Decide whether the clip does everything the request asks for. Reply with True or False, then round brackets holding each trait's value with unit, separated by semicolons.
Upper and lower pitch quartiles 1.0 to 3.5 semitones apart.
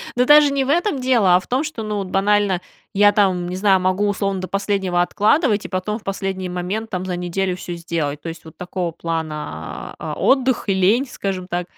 True (3.0 semitones)